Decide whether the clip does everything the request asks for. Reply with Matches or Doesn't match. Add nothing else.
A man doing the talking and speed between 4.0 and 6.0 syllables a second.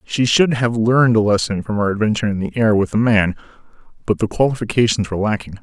Doesn't match